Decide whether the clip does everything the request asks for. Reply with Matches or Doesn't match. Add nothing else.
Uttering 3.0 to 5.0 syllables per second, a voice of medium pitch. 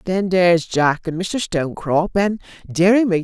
Matches